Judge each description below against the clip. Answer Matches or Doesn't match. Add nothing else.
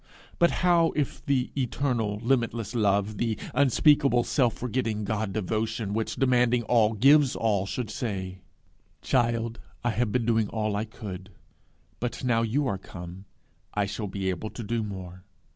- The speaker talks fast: Doesn't match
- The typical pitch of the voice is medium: Doesn't match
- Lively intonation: Doesn't match